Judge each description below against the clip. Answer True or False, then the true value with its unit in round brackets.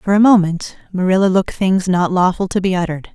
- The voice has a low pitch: False (185 Hz)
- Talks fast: True (210 wpm)